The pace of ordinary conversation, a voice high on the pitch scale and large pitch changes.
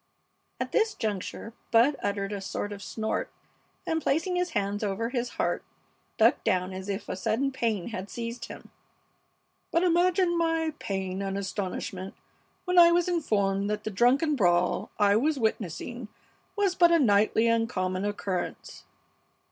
Yes: average, 155 wpm; high, 220 Hz; wide, 8.1 semitones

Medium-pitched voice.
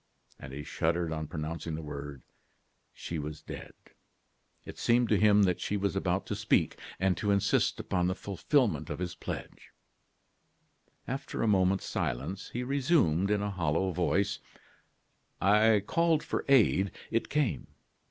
No: very low, 95 Hz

